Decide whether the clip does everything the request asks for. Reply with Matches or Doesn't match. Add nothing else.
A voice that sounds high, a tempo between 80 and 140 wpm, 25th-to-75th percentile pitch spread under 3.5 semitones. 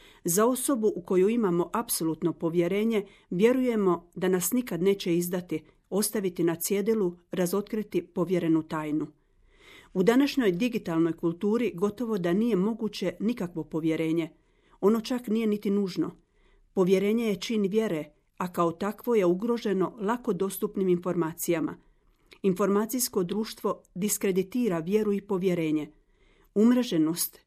Doesn't match